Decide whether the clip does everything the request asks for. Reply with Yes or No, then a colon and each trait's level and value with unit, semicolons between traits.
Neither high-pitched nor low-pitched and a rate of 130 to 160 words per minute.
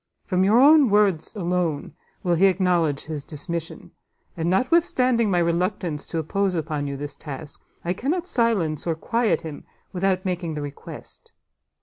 Yes: medium, 180 Hz; average, 150 wpm